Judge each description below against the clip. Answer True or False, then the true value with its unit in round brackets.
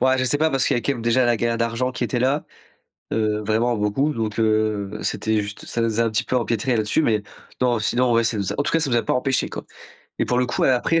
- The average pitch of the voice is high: False (115 Hz)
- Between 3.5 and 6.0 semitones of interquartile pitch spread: False (2.8 semitones)